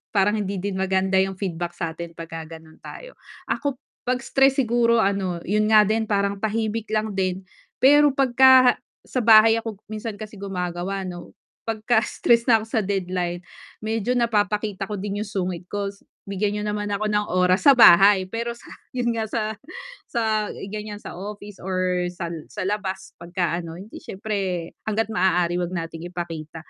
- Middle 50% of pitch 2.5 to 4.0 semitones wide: Yes, average, 3.3 semitones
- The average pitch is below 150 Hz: No, high, 205 Hz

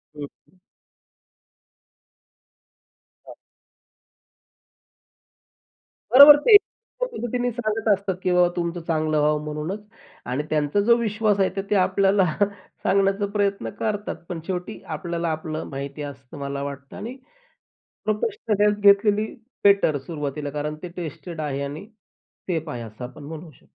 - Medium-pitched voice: Yes, medium, 175 Hz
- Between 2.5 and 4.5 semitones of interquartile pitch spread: No, wide, 5.6 semitones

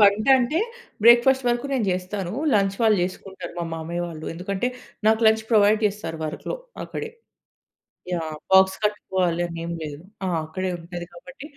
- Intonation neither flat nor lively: Yes, average, 4.1 semitones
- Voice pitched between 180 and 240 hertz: Yes, high, 190 Hz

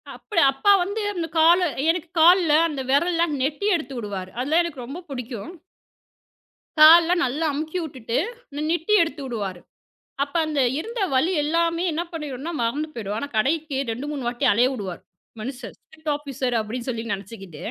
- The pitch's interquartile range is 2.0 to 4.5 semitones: No, average, 5.2 semitones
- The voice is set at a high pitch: Yes, very high, 285 Hz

